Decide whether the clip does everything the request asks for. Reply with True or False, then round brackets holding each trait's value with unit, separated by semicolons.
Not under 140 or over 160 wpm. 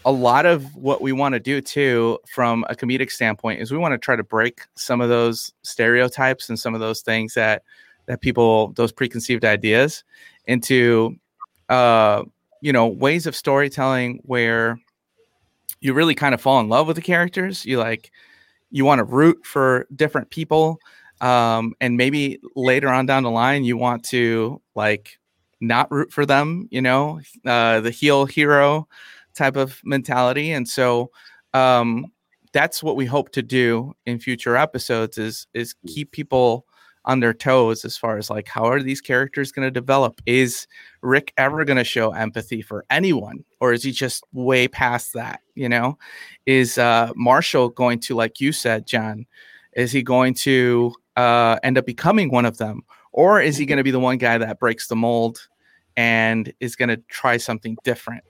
False (180 wpm)